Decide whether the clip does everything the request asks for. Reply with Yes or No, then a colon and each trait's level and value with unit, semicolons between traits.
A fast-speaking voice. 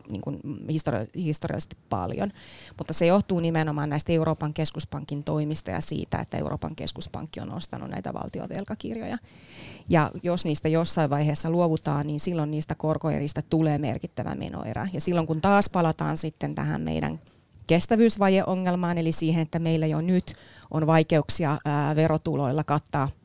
No: average, 140 wpm